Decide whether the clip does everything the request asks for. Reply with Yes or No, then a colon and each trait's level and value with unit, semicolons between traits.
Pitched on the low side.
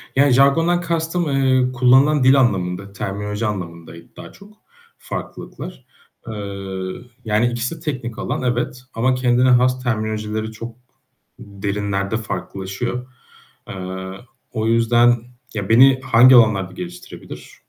Yes: low, 115 Hz